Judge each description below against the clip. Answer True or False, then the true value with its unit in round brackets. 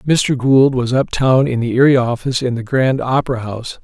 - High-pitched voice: False (125 Hz)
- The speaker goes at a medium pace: False (220 wpm)